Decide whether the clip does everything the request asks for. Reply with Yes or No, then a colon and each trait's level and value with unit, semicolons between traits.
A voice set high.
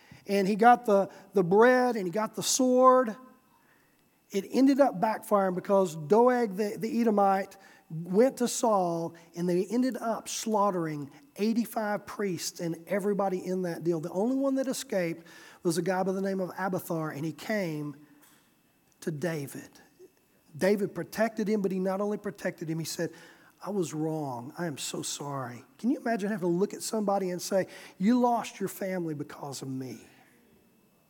Yes: high, 195 Hz